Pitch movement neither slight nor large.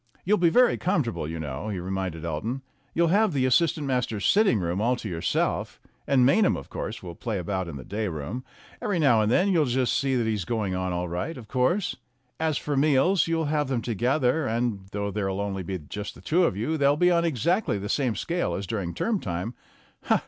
No: wide, 8.4 semitones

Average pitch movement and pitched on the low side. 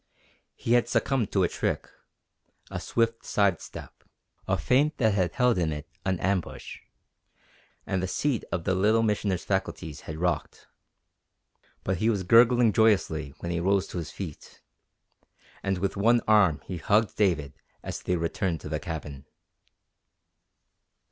Yes: average, 4.5 semitones; very low, 95 Hz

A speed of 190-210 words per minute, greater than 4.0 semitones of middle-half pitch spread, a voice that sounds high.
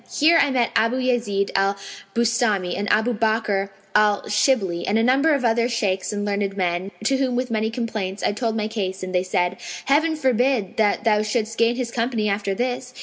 No: average, 200 wpm; average, 3.6 semitones; high, 220 Hz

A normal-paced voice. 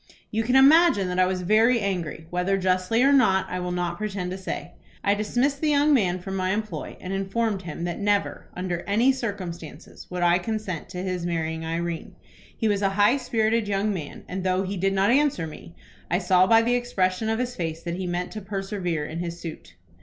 No: fast, 215 wpm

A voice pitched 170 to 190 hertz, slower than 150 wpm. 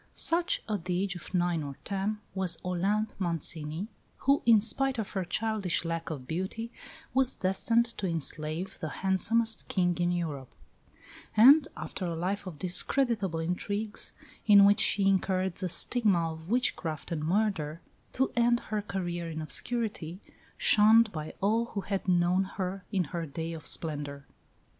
No: medium, 185 Hz; average, 155 wpm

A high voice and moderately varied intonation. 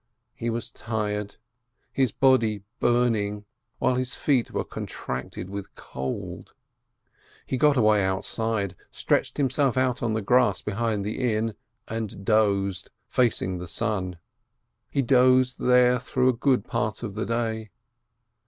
No: low, 115 Hz; average, 3.3 semitones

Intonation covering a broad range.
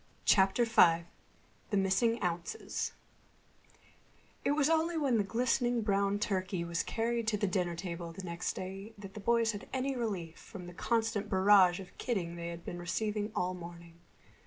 No: average, 4.5 semitones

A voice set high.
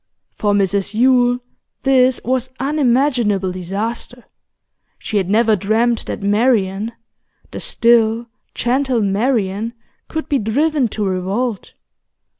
Yes: high, 230 Hz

